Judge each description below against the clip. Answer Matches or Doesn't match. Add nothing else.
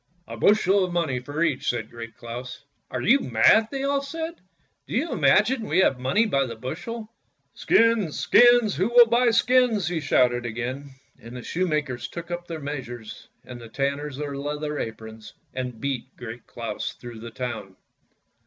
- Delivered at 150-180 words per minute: Doesn't match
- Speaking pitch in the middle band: Matches